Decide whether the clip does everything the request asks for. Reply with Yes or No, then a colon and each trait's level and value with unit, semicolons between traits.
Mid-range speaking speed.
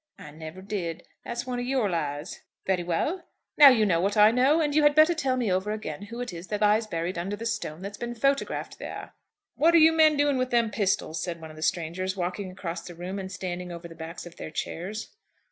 No: fast, 240 wpm